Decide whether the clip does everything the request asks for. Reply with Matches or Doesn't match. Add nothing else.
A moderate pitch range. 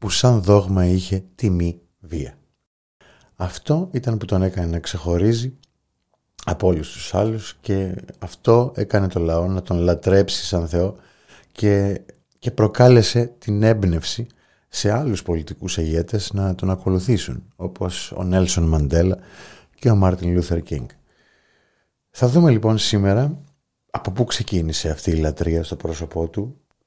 Matches